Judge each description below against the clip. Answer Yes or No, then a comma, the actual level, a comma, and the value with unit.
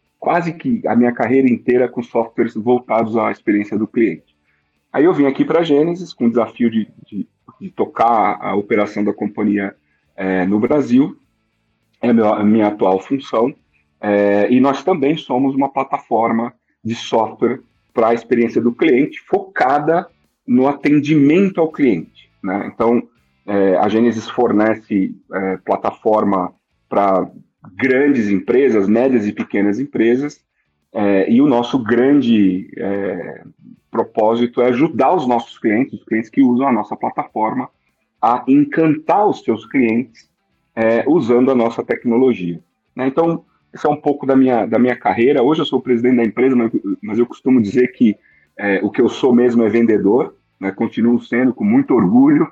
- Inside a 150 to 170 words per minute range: Yes, average, 160 wpm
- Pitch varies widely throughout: No, average, 4.3 semitones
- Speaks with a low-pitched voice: Yes, low, 120 Hz